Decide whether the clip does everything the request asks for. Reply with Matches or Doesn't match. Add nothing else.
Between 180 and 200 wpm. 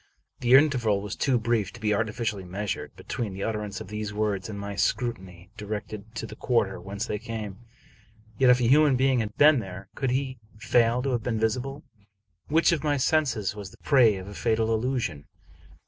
Matches